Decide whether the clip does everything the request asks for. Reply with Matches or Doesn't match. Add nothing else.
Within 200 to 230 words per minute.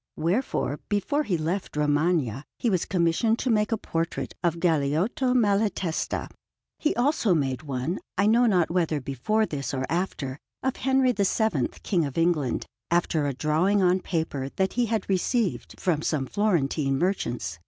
Doesn't match